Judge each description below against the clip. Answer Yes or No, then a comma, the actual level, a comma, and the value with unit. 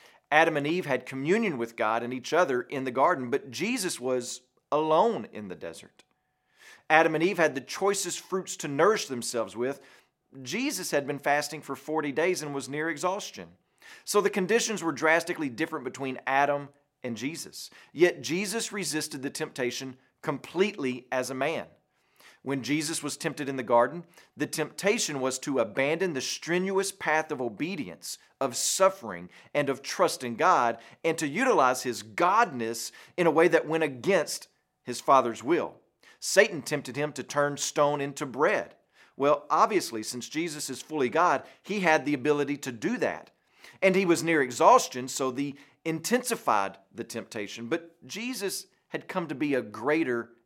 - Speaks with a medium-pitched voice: Yes, medium, 145 Hz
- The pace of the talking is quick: No, average, 165 wpm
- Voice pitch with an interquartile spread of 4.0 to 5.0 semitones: Yes, average, 4.5 semitones